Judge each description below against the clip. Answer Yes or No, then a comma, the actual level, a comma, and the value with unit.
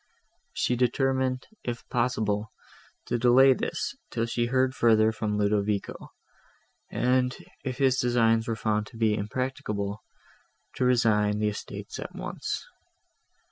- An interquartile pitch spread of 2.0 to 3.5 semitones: Yes, average, 3.1 semitones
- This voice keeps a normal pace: No, slow, 125 wpm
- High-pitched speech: No, low, 115 Hz